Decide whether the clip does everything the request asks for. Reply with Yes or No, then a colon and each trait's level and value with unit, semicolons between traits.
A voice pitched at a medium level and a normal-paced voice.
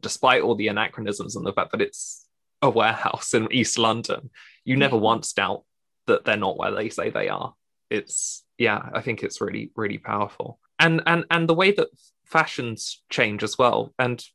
Yes: medium, 165 Hz; average, 190 wpm